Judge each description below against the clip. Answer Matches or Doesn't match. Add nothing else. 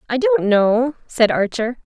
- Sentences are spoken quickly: Doesn't match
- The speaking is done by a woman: Matches